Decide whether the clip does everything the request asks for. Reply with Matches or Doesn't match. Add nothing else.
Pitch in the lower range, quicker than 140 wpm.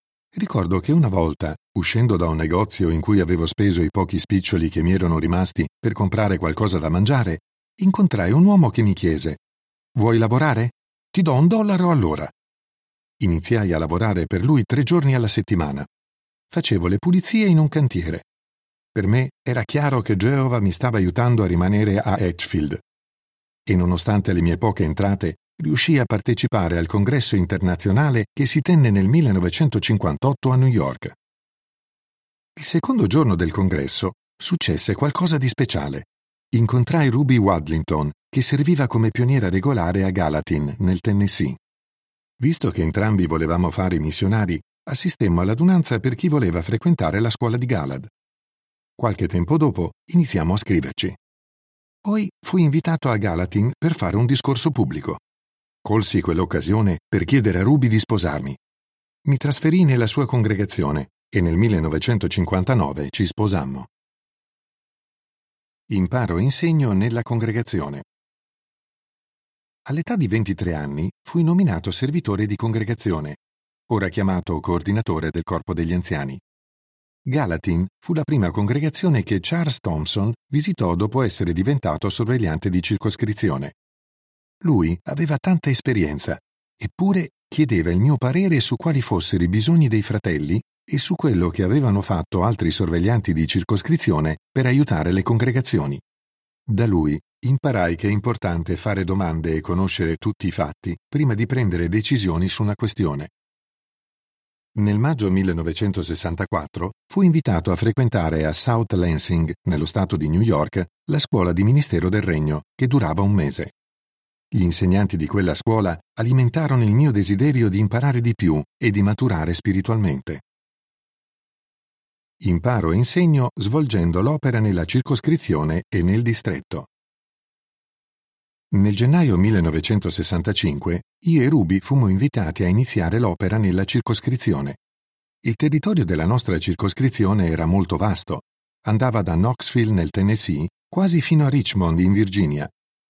Doesn't match